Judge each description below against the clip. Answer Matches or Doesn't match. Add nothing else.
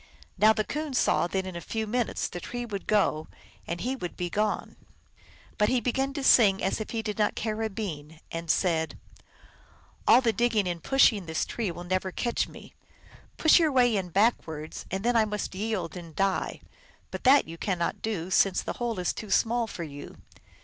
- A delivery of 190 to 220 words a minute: Matches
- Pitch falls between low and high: Doesn't match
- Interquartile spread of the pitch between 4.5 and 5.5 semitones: Matches